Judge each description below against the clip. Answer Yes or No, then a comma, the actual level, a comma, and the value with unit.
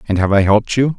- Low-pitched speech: Yes, low, 110 Hz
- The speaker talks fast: Yes, fast, 305 wpm